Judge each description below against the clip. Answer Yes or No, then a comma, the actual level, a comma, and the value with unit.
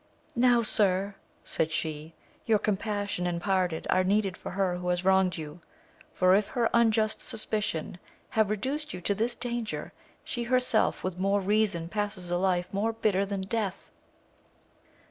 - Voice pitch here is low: No, high, 195 Hz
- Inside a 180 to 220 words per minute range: No, average, 160 wpm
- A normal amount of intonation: Yes, average, 3.3 semitones